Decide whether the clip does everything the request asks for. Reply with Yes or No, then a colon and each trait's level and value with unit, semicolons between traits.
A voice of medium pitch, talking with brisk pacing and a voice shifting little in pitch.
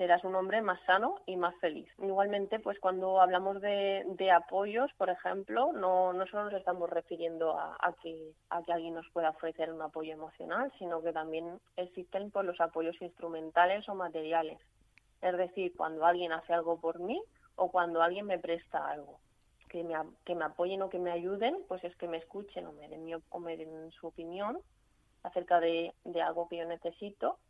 Yes: medium, 175 Hz; fast, 195 wpm; narrow, 2.2 semitones